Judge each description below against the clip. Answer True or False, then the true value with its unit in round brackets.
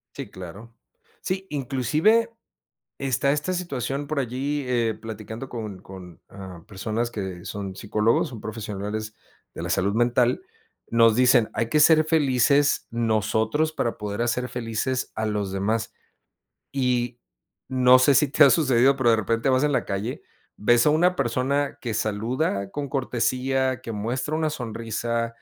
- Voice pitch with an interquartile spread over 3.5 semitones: True (3.9 semitones)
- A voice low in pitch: True (120 Hz)